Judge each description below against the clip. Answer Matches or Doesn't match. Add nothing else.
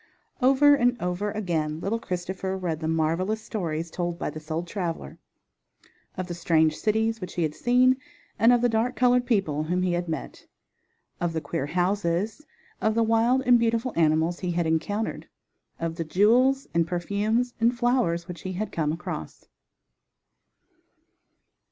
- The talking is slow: Doesn't match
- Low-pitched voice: Doesn't match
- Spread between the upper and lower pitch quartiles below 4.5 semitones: Doesn't match